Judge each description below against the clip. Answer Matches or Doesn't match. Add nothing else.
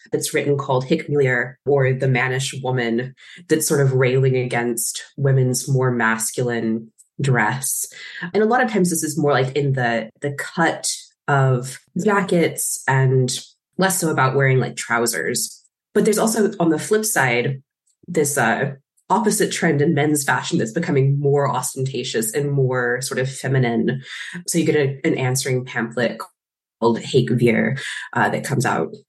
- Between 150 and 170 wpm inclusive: Matches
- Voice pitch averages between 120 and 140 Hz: Matches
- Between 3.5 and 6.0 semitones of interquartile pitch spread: Matches